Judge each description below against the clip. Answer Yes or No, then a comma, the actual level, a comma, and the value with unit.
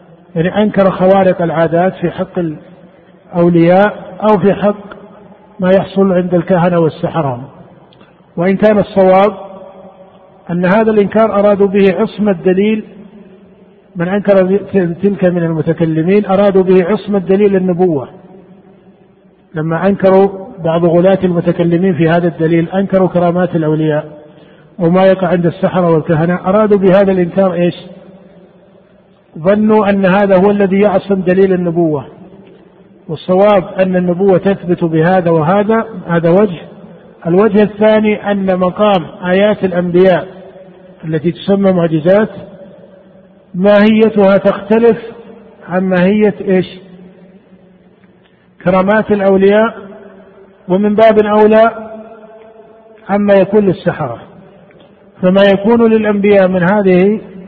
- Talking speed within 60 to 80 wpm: No, average, 100 wpm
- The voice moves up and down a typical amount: No, narrow, 1.9 semitones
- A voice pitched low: No, high, 190 Hz